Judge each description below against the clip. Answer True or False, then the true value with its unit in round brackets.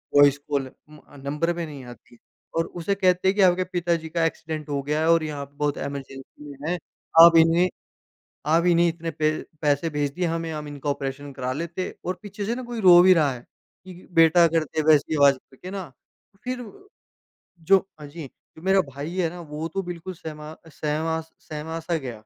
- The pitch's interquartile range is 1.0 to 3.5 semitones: True (3.1 semitones)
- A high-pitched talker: False (160 Hz)